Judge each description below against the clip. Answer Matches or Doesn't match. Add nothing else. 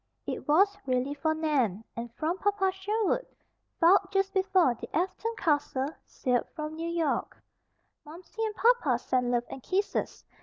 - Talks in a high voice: Matches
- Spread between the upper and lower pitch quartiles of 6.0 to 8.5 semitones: Matches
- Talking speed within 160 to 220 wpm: Doesn't match